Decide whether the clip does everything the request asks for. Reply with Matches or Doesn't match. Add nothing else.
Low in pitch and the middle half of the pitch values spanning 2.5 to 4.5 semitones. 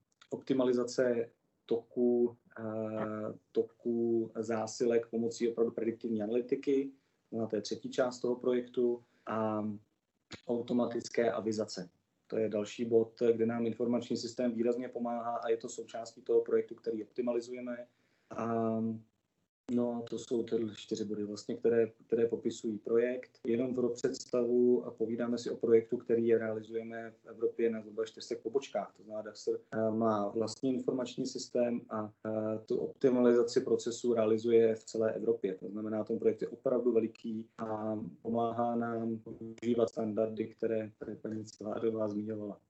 Doesn't match